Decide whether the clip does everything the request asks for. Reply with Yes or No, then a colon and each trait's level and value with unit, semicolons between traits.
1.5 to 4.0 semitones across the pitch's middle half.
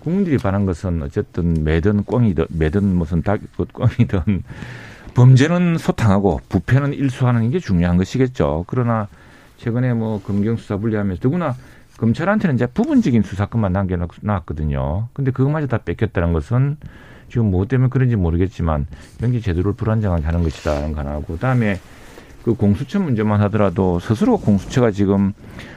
No: wide, 5.6 semitones